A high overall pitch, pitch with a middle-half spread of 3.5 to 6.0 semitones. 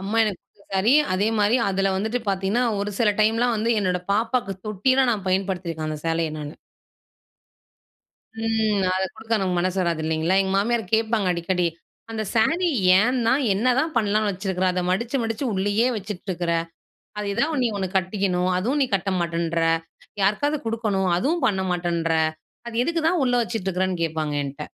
Yes: high, 200 Hz; average, 3.8 semitones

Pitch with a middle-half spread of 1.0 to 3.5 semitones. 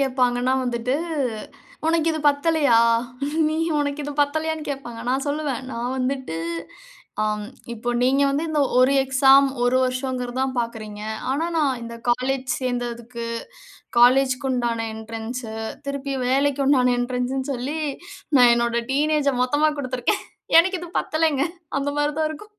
Yes: average, 2.8 semitones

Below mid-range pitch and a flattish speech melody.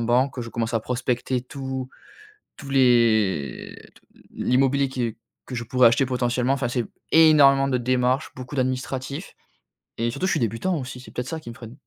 Yes: low, 125 Hz; narrow, 2.3 semitones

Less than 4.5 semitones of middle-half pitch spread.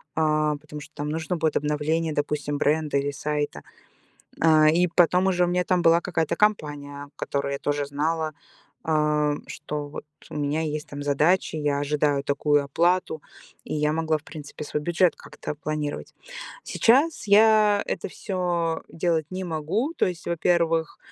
Yes: average, 2.8 semitones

